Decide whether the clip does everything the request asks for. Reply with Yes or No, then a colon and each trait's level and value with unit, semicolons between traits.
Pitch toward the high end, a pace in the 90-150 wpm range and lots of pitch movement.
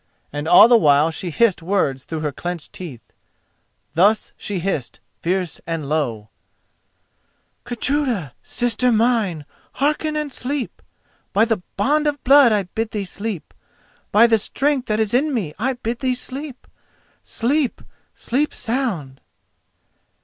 Yes: high, 220 Hz; slow, 135 wpm; wide, 7.0 semitones